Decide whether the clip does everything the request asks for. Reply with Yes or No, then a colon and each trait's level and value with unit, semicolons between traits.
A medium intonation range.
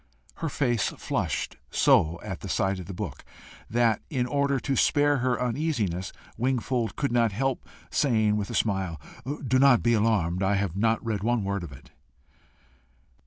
Yes: average, 4.6 semitones